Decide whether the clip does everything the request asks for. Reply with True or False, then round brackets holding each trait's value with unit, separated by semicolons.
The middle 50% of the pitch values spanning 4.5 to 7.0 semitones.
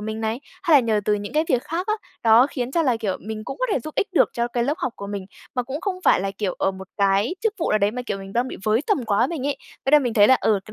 True (5.1 semitones)